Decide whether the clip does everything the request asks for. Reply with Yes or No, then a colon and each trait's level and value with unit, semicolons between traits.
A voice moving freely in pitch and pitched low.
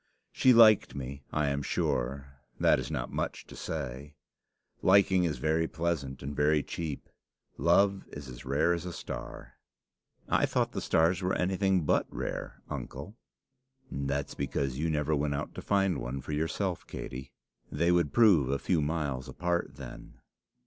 No: average, 4.1 semitones; very low, 75 Hz